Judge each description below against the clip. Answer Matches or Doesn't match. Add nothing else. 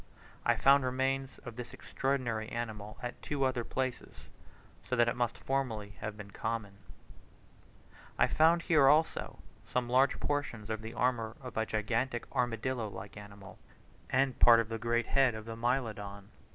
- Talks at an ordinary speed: Matches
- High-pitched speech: Doesn't match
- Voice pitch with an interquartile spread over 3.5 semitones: Doesn't match